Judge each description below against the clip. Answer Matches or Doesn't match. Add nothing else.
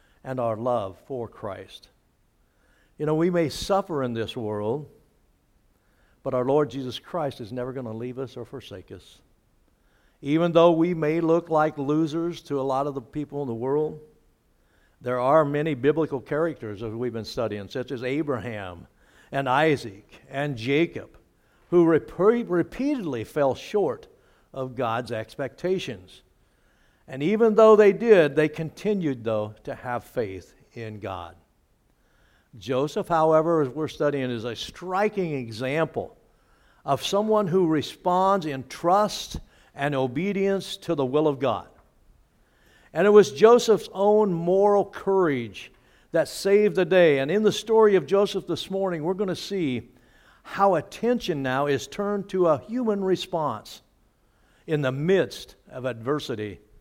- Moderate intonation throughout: Doesn't match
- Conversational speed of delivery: Matches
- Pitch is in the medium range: Matches